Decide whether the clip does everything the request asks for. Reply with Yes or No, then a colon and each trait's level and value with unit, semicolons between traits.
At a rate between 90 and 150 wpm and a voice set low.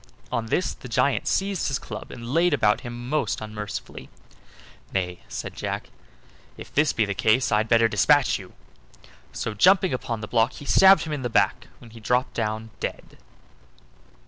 No: average, 170 wpm; low, 120 Hz